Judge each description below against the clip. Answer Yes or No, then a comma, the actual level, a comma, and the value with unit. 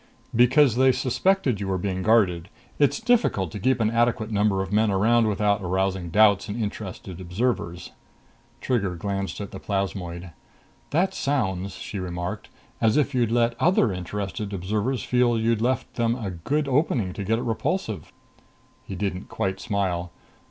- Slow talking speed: No, average, 160 wpm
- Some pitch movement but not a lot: Yes, average, 4.1 semitones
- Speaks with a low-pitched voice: Yes, low, 105 Hz